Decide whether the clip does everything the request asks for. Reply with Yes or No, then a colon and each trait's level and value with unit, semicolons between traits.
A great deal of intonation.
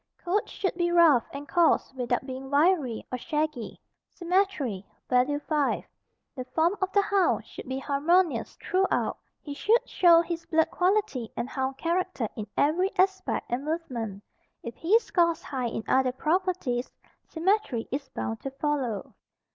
Yes: wide, 5.7 semitones